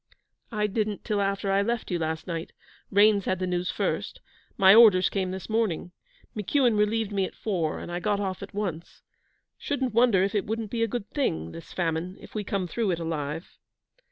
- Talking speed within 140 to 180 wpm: No, average, 200 wpm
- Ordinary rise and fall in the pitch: Yes, average, 3.2 semitones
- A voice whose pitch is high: Yes, high, 195 Hz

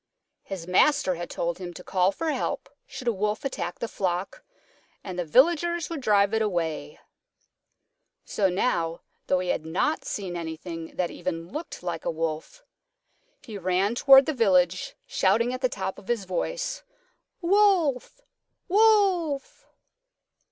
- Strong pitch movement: Yes, wide, 8.9 semitones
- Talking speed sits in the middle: Yes, average, 145 wpm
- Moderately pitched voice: No, high, 200 Hz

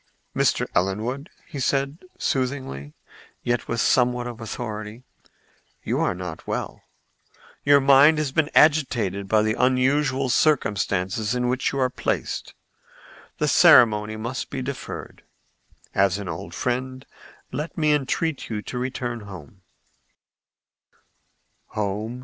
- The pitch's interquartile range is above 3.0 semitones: Yes, average, 4.4 semitones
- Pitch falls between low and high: No, low, 125 Hz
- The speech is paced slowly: Yes, slow, 120 wpm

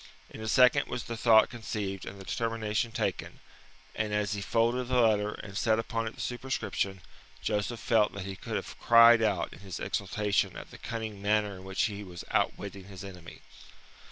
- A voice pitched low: Yes, low, 105 Hz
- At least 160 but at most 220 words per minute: Yes, average, 190 wpm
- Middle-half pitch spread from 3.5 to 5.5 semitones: No, narrow, 2.6 semitones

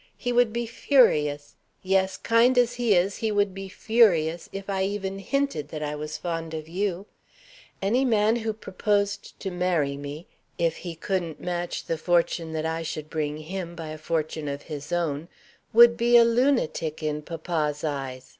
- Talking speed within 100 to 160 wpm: No, average, 175 wpm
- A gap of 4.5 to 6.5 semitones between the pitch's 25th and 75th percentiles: Yes, average, 5.1 semitones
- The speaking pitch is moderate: Yes, medium, 175 Hz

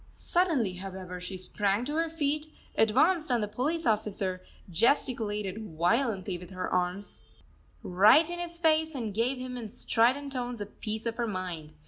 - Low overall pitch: No, high, 225 Hz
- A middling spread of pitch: No, wide, 6.6 semitones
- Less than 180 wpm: Yes, average, 160 wpm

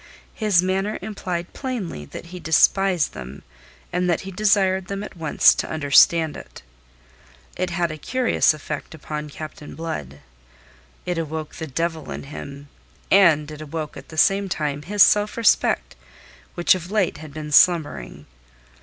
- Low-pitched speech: No, medium, 165 Hz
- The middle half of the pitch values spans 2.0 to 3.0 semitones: No, average, 4.1 semitones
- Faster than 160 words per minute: No, average, 155 wpm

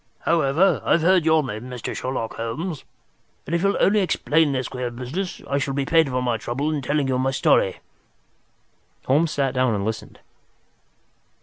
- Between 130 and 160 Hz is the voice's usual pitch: Yes, low, 135 Hz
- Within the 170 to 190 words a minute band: Yes, average, 175 wpm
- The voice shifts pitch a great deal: No, average, 4.2 semitones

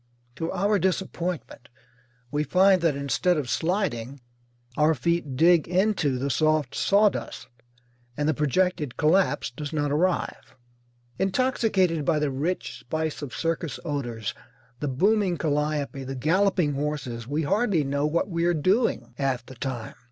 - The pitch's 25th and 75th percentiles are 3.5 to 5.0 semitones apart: Yes, average, 4.5 semitones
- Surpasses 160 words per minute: No, average, 140 wpm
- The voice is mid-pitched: Yes, medium, 155 Hz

